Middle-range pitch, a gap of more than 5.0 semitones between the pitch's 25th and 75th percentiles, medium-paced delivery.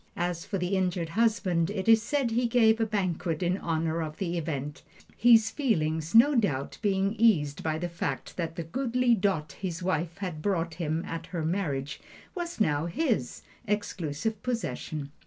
Yes: medium, 180 Hz; wide, 5.4 semitones; average, 170 wpm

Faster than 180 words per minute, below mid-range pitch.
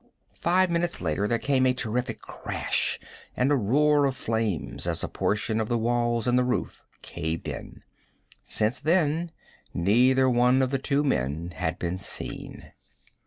No: average, 160 wpm; low, 125 Hz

